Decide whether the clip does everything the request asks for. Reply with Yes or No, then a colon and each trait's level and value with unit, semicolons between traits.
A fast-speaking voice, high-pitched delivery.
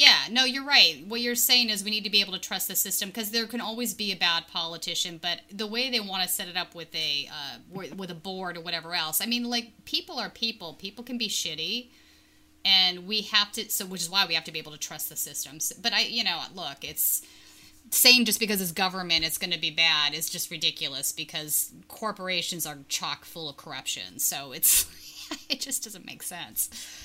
Yes: fast, 230 wpm; high, 195 Hz